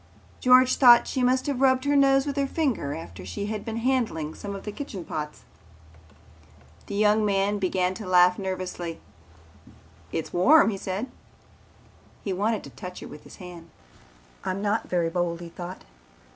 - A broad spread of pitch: Yes, wide, 5.9 semitones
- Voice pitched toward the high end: Yes, high, 200 Hz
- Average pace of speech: Yes, average, 170 wpm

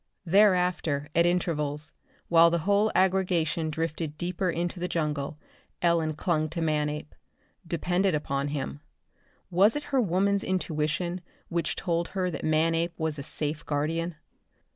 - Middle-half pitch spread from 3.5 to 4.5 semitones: No, average, 2.8 semitones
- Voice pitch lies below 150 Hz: No, medium, 165 Hz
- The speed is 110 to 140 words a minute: Yes, slow, 135 wpm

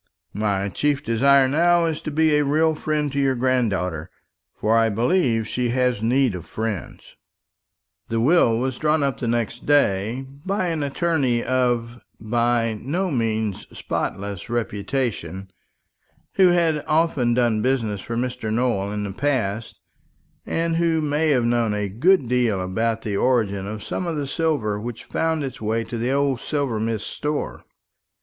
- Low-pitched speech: Yes, low, 120 Hz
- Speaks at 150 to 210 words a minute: Yes, average, 155 wpm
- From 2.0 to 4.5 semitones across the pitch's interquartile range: No, average, 5.0 semitones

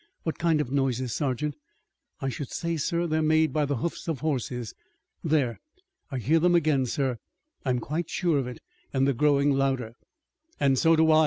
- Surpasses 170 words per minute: Yes, average, 190 wpm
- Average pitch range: Yes, average, 3.3 semitones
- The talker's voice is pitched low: No, medium, 145 Hz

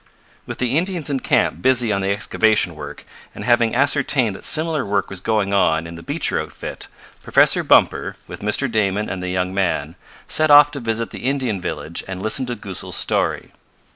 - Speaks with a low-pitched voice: Yes, low, 110 Hz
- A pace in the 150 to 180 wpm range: No, average, 190 wpm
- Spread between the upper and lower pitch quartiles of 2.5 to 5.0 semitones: No, wide, 5.4 semitones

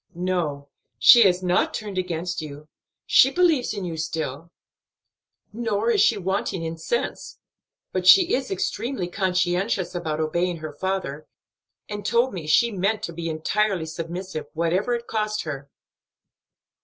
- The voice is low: No, medium, 180 Hz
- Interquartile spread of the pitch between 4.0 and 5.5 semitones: Yes, average, 4.5 semitones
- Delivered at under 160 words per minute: Yes, average, 145 wpm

